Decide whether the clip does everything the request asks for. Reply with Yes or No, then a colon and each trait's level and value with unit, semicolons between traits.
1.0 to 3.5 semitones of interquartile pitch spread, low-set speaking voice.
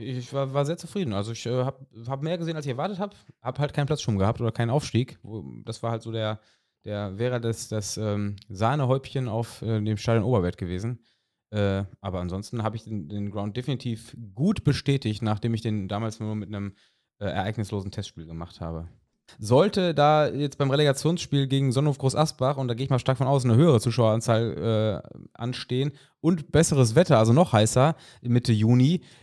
No: average, 4.2 semitones; low, 120 Hz